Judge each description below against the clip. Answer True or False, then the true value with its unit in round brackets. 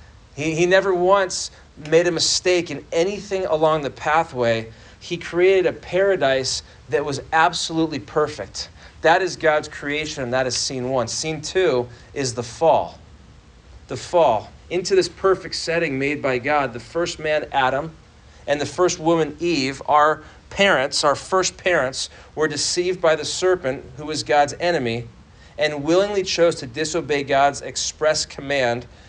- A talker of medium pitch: True (155 Hz)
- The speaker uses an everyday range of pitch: True (3.9 semitones)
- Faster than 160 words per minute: False (155 wpm)